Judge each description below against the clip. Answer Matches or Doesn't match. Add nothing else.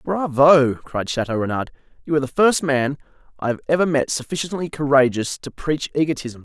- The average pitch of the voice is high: Doesn't match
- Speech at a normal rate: Matches